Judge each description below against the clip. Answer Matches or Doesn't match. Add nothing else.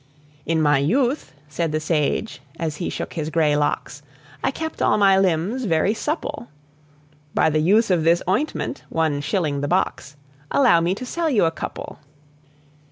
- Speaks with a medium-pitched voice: Matches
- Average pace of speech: Matches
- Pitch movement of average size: Doesn't match